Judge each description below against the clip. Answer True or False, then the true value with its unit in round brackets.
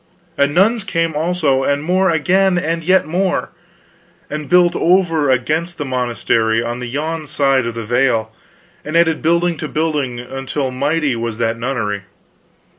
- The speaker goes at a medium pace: True (155 wpm)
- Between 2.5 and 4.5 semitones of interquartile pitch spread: False (5.1 semitones)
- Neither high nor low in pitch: True (150 Hz)